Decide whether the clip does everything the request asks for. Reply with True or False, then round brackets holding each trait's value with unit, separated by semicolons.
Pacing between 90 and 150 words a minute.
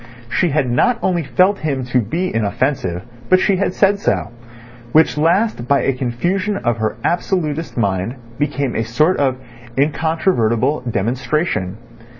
True (145 wpm)